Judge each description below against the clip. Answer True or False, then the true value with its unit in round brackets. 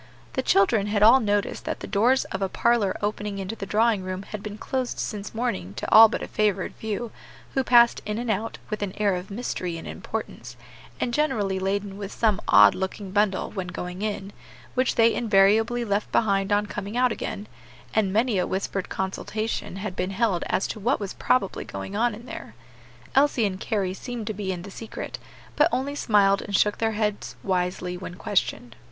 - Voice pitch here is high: True (205 Hz)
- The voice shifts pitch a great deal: False (2.8 semitones)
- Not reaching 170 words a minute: False (195 wpm)